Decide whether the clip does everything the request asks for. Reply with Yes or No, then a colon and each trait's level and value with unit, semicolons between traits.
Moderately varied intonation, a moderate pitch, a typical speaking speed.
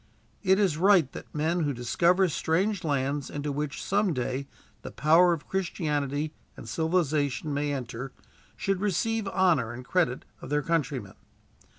Yes: average, 4.5 semitones; medium, 155 Hz; average, 150 wpm